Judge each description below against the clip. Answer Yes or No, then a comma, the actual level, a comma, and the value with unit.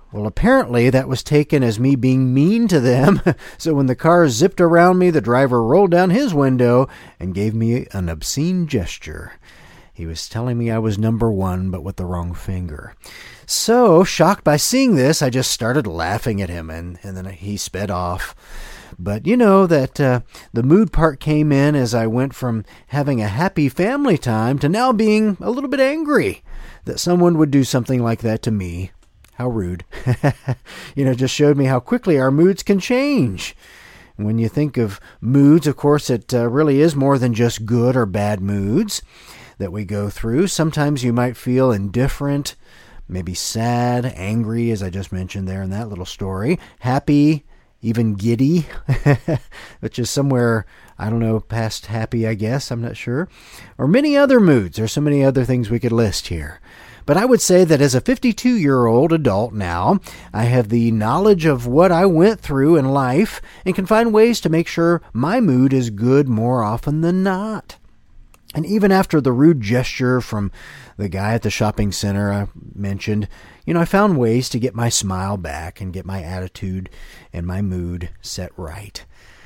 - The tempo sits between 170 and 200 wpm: Yes, average, 190 wpm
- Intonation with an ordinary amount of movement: No, wide, 7.0 semitones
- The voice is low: Yes, low, 125 Hz